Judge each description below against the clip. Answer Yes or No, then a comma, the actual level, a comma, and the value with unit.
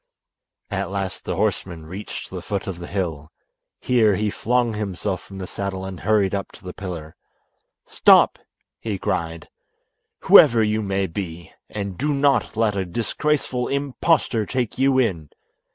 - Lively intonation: No, average, 3.8 semitones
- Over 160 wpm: No, average, 150 wpm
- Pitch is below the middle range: Yes, low, 100 Hz